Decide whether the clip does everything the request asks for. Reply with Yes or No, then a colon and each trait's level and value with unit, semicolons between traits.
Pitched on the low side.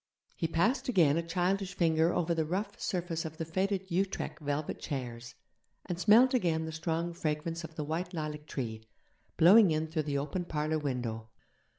No: medium, 165 Hz